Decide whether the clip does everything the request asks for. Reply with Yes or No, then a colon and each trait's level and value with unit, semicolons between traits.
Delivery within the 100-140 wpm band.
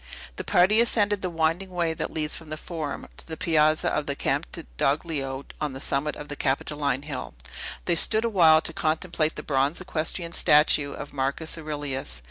No: average, 175 wpm